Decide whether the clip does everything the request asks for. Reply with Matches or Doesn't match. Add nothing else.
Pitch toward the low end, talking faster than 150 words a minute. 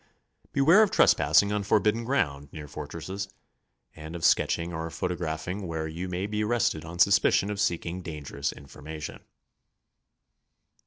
Doesn't match